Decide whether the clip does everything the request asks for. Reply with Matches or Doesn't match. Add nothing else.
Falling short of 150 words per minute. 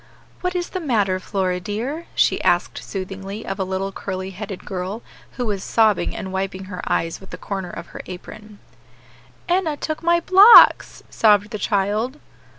Doesn't match